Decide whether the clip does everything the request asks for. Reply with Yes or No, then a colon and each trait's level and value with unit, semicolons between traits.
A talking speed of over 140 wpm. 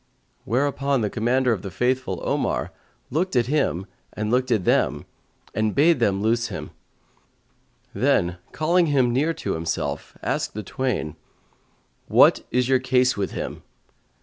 No: slow, 135 wpm